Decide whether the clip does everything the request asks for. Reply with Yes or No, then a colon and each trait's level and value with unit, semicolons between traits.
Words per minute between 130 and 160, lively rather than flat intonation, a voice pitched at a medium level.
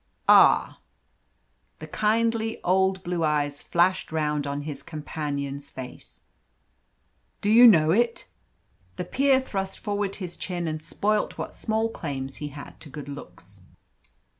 Yes: slow, 135 wpm; wide, 6.3 semitones; medium, 175 Hz